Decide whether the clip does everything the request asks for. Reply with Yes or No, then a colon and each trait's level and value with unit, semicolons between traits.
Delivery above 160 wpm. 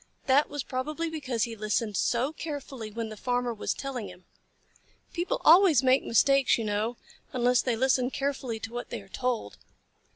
Yes: average, 170 wpm